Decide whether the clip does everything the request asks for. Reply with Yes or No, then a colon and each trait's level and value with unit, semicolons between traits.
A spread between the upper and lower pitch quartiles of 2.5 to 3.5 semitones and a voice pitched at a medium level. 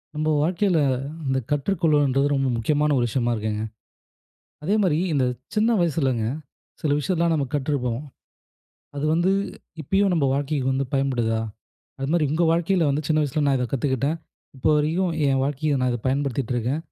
Yes: average, 3.2 semitones; medium, 145 Hz